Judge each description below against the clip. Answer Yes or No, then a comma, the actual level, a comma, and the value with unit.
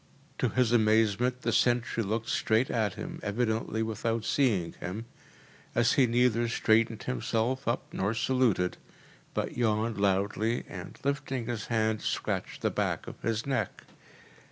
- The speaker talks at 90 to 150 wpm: Yes, average, 140 wpm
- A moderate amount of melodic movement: No, narrow, 2.0 semitones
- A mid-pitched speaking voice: No, low, 115 Hz